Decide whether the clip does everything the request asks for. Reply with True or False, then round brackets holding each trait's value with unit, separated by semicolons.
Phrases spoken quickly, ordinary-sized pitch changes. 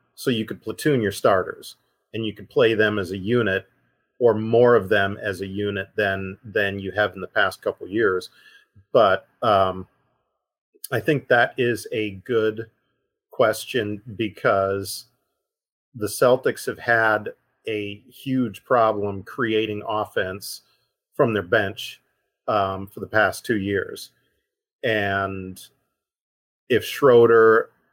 False (135 wpm; 3.7 semitones)